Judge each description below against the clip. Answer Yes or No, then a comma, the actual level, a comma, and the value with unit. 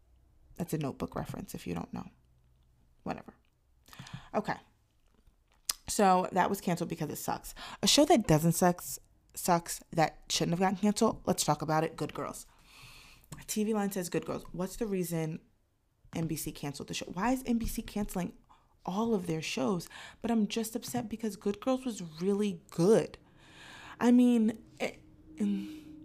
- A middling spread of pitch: No, wide, 5.8 semitones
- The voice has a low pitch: No, high, 190 Hz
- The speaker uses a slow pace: No, average, 155 wpm